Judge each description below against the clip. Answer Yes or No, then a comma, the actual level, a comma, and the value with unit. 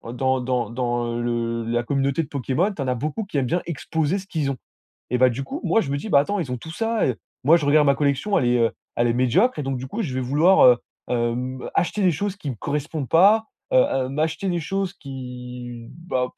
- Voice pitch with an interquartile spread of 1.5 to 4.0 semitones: No, average, 5.2 semitones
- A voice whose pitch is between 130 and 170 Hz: Yes, medium, 140 Hz